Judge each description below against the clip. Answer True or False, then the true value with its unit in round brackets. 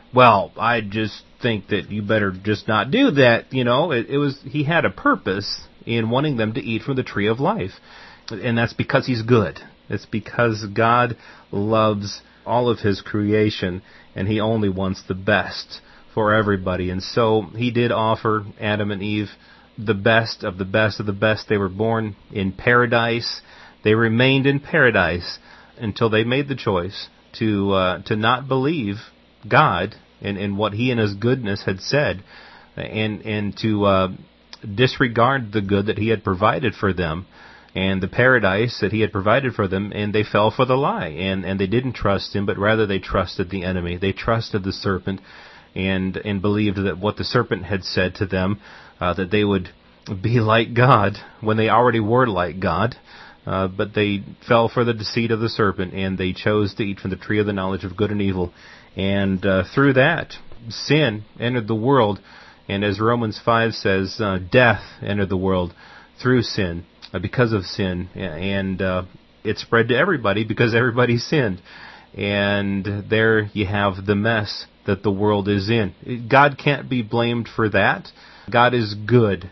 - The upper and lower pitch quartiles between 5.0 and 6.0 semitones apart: False (3.0 semitones)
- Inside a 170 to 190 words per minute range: True (185 wpm)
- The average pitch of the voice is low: True (105 Hz)